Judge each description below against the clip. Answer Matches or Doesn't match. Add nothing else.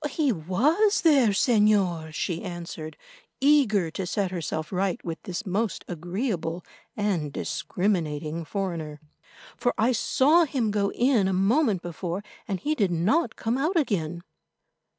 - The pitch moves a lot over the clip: Matches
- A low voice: Doesn't match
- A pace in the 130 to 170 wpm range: Matches